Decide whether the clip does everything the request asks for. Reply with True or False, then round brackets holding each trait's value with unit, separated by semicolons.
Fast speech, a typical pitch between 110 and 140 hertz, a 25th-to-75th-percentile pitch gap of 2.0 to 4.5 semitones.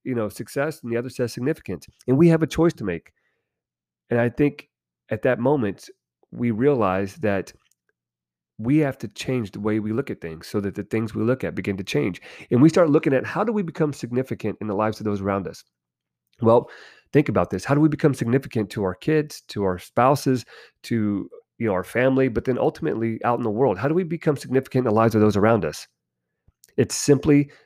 False (220 wpm; 115 Hz; 5.4 semitones)